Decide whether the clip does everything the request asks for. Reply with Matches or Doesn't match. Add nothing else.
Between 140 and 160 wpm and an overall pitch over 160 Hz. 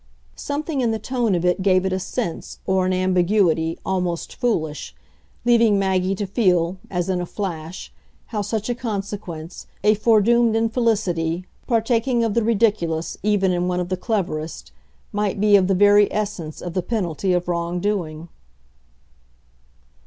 Matches